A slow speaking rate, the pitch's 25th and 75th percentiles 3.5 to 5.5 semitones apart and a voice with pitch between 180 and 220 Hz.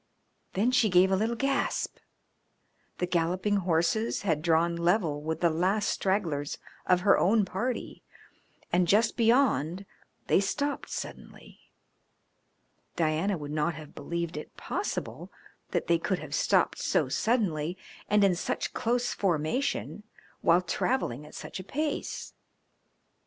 Yes: slow, 130 wpm; average, 4.7 semitones; medium, 185 Hz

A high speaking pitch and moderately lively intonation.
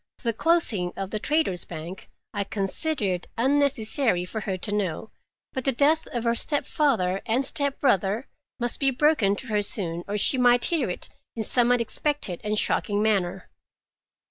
No: high, 225 Hz; wide, 5.7 semitones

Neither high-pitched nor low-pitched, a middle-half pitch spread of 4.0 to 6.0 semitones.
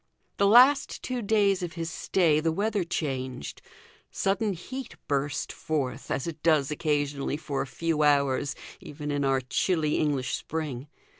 Yes: medium, 155 Hz; average, 4.6 semitones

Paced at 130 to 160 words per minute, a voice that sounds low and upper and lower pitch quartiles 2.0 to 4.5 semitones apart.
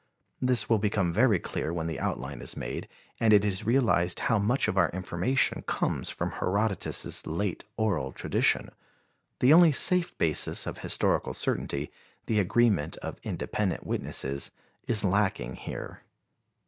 No: average, 145 wpm; low, 100 Hz; average, 4.9 semitones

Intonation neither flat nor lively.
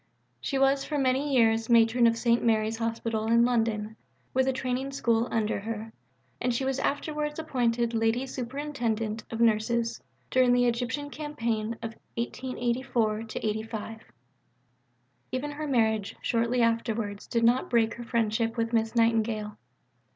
No: narrow, 2.2 semitones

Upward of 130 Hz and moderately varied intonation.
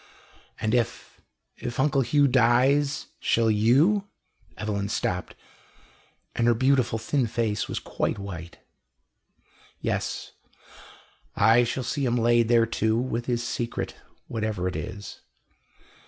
No: low, 120 Hz; average, 3.0 semitones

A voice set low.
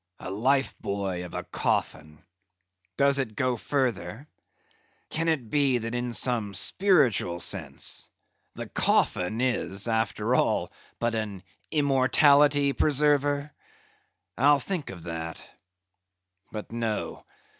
Yes: low, 120 Hz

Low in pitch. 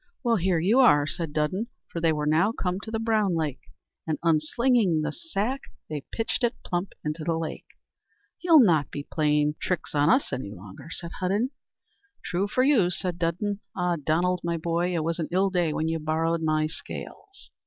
No: medium, 170 Hz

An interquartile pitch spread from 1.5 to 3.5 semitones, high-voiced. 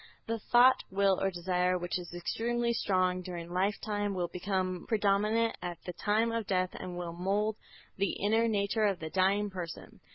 Yes: average, 2.8 semitones; high, 195 Hz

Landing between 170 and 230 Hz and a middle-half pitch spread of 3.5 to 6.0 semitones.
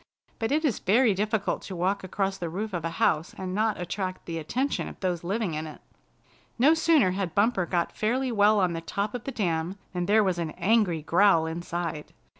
Yes: high, 190 Hz; average, 4.0 semitones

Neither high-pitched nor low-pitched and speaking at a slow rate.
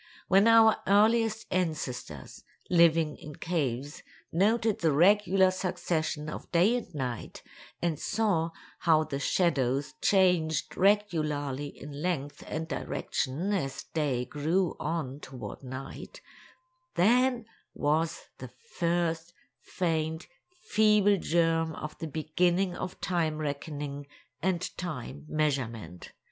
Yes: medium, 165 Hz; slow, 110 wpm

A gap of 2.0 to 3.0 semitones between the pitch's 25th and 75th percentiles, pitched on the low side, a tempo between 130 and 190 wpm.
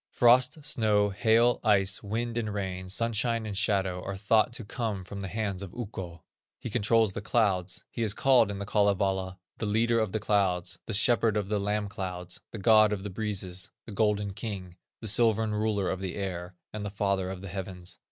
No: narrow, 2.6 semitones; low, 105 Hz; average, 200 wpm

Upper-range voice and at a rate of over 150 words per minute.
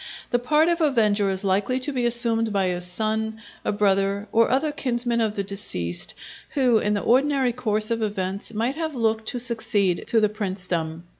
Yes: high, 220 Hz; average, 190 wpm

